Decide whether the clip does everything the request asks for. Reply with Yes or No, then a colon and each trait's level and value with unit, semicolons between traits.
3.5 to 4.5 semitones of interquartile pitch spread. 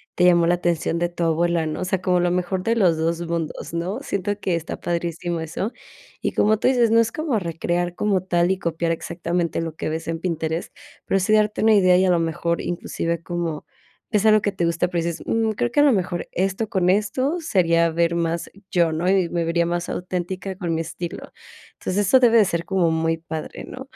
No: narrow, 2.5 semitones